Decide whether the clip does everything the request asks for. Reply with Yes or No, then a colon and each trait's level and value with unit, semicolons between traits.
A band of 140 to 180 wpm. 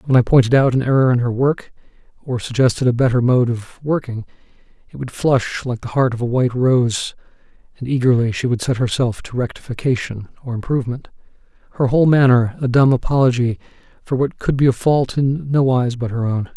No: average, 195 wpm